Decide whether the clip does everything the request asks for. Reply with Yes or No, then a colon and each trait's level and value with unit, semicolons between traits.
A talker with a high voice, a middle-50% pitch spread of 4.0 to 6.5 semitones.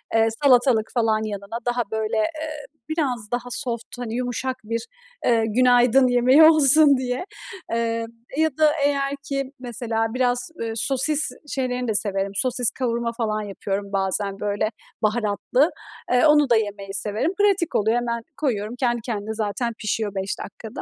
No: high, 240 Hz; average, 3.2 semitones